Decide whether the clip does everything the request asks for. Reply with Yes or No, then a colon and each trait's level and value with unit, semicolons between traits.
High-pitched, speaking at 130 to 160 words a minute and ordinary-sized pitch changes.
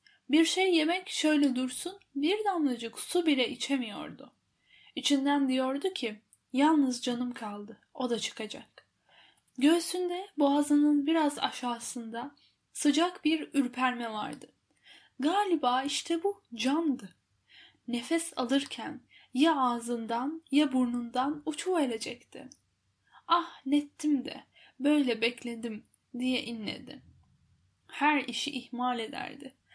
No: very high, 275 Hz; average, 100 wpm; average, 4.2 semitones